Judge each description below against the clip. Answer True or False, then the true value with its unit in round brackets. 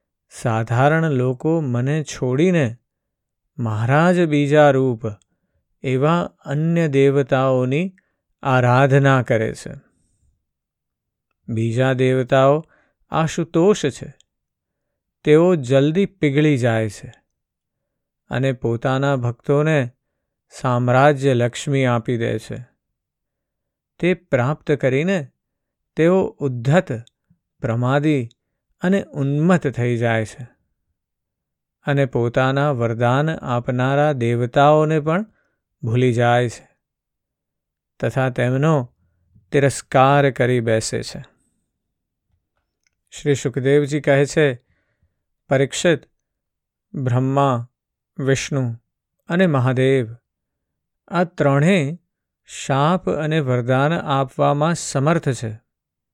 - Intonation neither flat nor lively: True (3.7 semitones)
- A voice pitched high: False (135 Hz)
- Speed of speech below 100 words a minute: True (80 wpm)